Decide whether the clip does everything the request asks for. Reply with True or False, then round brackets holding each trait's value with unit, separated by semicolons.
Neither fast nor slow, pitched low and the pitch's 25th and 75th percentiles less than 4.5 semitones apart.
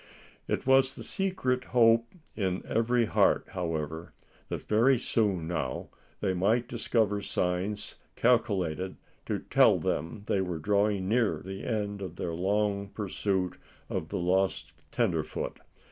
False (130 wpm; 100 Hz; 4.1 semitones)